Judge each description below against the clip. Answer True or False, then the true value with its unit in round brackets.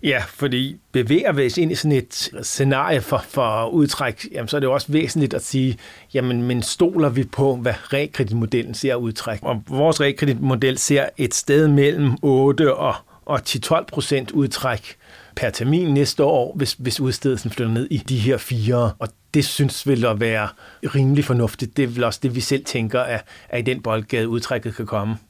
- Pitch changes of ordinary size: True (3.3 semitones)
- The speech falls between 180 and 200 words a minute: True (190 wpm)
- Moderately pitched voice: False (130 Hz)